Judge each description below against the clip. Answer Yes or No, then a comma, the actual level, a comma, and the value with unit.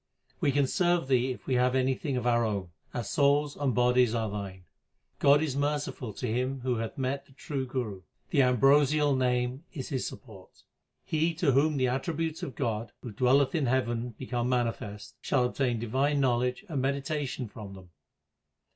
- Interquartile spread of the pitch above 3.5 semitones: No, average, 2.9 semitones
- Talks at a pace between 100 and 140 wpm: No, average, 180 wpm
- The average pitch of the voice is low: Yes, low, 130 Hz